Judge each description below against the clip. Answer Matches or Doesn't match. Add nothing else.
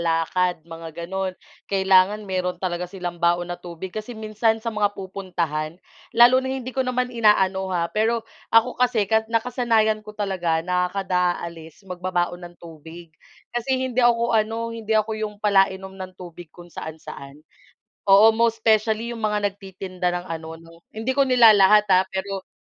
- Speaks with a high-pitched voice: Matches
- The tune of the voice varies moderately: Matches